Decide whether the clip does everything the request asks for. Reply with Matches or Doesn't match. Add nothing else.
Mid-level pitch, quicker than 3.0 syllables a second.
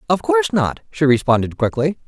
Matches